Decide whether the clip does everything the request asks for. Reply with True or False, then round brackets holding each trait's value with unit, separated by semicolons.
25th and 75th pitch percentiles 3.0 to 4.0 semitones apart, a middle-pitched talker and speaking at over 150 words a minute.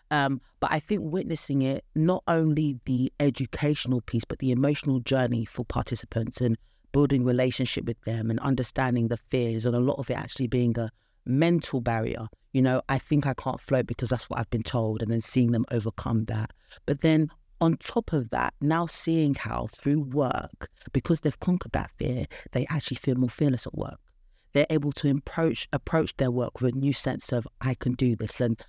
False (3.5 semitones; 130 Hz; 200 wpm)